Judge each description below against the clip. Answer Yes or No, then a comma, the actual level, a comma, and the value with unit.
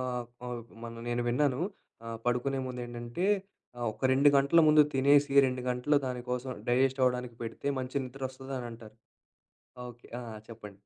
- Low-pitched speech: Yes, low, 125 Hz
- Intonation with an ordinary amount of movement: No, narrow, 2.0 semitones